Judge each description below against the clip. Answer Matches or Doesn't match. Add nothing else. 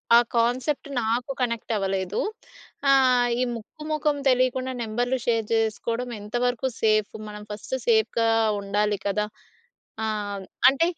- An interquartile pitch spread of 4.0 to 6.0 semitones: Doesn't match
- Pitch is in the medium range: Doesn't match